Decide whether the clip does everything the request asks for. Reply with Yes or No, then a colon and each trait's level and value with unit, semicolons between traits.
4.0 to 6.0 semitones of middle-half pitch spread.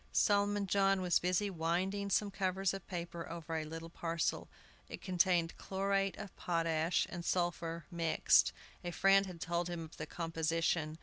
No: average, 2.7 semitones